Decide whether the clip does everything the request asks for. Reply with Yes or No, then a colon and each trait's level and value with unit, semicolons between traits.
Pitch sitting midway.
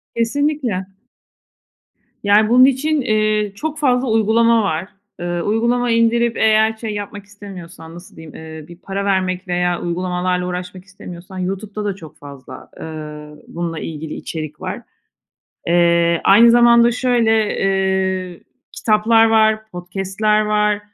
No: high, 200 Hz